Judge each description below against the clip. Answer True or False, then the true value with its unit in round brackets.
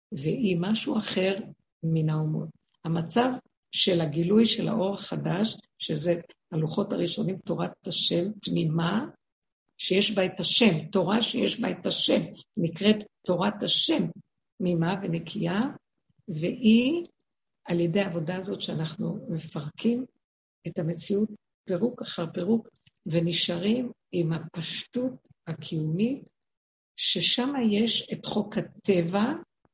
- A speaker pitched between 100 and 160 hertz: False (190 Hz)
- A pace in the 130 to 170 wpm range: False (105 wpm)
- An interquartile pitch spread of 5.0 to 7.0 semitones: False (4.4 semitones)